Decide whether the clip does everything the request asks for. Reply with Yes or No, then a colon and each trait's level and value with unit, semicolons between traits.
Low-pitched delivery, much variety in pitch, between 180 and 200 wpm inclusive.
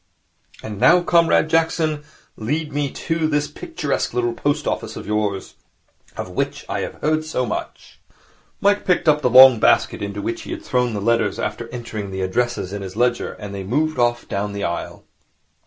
Yes: low, 120 Hz; wide, 6.7 semitones; average, 185 wpm